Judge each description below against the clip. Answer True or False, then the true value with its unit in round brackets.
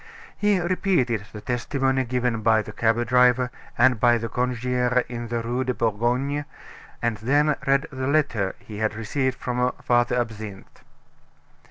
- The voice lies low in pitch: True (125 Hz)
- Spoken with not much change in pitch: True (2.3 semitones)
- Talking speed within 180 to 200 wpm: False (150 wpm)